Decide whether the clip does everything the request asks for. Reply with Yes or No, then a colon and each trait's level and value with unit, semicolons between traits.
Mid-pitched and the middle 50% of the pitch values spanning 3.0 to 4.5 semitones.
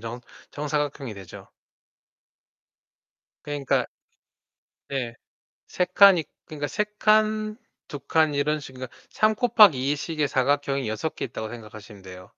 No: medium, 145 Hz; average, 5.1 semitones